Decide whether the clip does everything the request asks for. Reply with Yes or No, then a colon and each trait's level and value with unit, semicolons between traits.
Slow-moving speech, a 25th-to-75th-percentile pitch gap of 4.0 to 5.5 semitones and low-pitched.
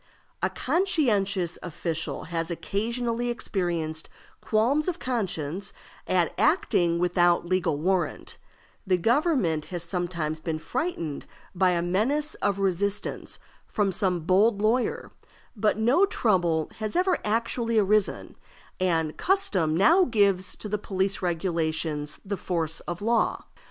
No: slow, 120 wpm; average, 5.1 semitones; high, 190 Hz